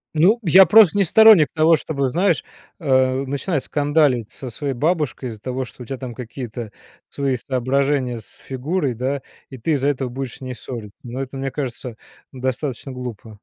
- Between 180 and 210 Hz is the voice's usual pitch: No, low, 135 Hz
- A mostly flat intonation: No, average, 3.0 semitones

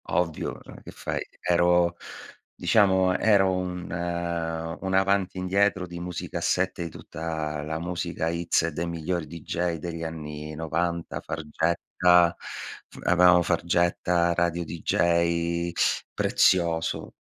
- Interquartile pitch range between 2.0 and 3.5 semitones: No, narrow, 1.3 semitones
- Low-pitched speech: Yes, very low, 85 Hz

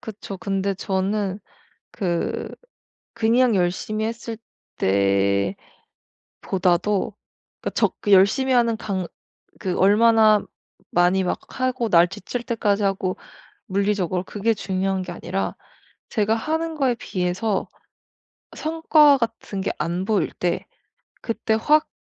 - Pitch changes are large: No, average, 3.6 semitones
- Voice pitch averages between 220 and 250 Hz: No, high, 200 Hz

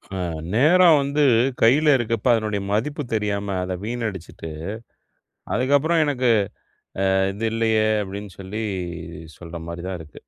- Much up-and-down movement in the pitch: Yes, wide, 6.1 semitones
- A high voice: No, low, 110 Hz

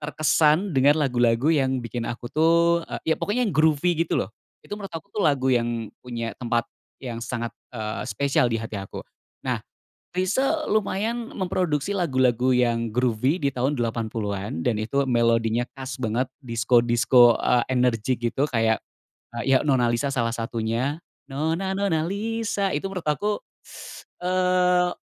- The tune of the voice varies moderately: No, wide, 6.2 semitones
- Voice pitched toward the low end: Yes, low, 130 Hz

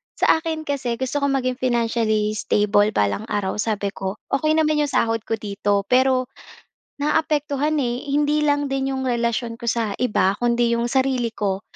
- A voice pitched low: No, high, 240 Hz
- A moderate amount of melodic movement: Yes, average, 4.5 semitones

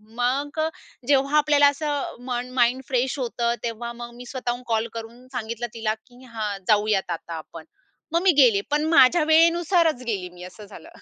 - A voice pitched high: Yes, high, 245 Hz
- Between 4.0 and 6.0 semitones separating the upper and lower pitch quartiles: Yes, average, 4.3 semitones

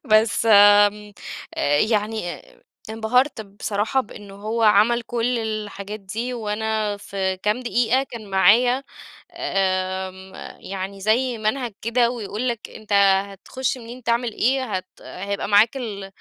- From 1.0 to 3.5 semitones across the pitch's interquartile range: Yes, average, 2.9 semitones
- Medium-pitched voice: No, high, 215 Hz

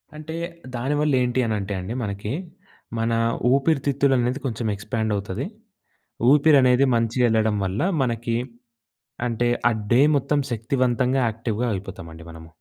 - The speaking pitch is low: Yes, low, 120 Hz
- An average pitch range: Yes, average, 3.6 semitones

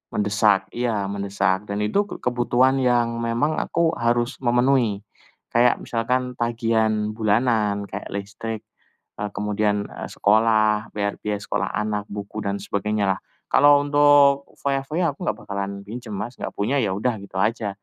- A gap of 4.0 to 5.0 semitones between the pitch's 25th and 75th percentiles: No, average, 3.1 semitones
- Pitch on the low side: Yes, low, 110 Hz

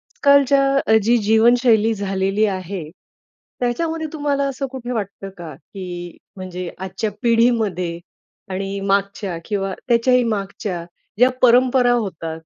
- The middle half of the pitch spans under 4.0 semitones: No, average, 4.4 semitones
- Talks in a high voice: Yes, high, 215 Hz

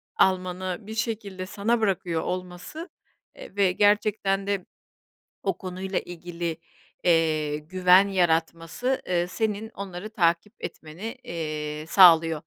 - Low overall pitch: No, medium, 185 Hz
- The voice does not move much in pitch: No, average, 3.1 semitones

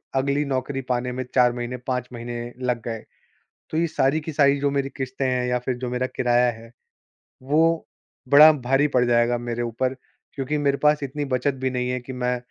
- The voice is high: No, low, 130 Hz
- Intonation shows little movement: Yes, narrow, 2.2 semitones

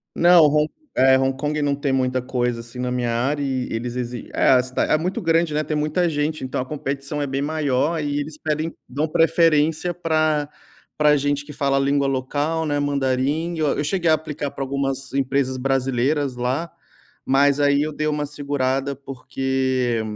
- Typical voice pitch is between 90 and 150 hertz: Yes, medium, 140 Hz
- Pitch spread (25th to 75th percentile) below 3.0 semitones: Yes, narrow, 2.6 semitones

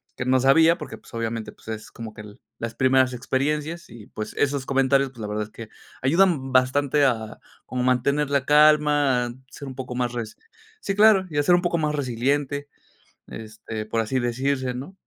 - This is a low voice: Yes, low, 130 Hz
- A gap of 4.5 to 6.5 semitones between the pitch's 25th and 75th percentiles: No, average, 3.8 semitones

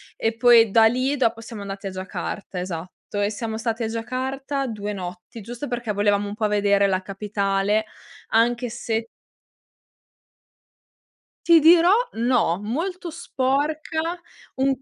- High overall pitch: Yes, high, 225 Hz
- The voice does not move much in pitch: No, average, 4.3 semitones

